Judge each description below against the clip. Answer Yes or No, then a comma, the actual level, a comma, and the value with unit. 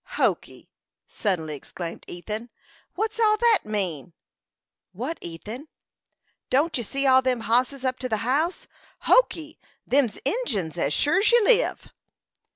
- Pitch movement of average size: No, wide, 8.0 semitones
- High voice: Yes, very high, 255 Hz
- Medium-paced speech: No, slow, 130 wpm